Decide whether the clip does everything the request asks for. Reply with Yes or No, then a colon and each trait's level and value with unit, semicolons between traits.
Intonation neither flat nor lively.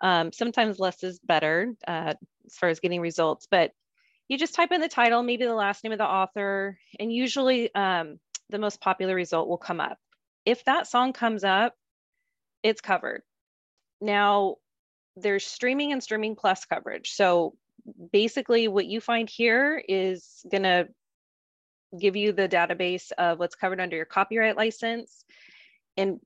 Yes: average, 4.2 semitones